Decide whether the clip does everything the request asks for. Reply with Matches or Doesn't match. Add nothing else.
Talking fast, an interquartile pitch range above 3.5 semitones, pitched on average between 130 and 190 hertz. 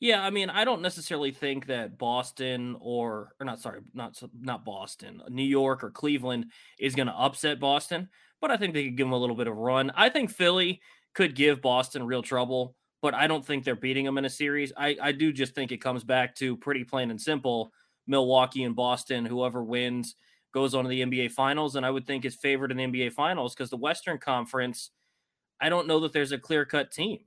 Doesn't match